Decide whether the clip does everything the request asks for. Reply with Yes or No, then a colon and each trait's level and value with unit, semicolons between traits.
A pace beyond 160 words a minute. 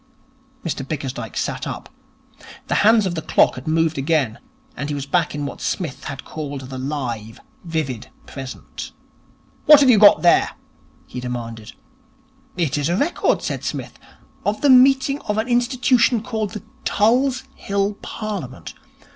No: average, 155 wpm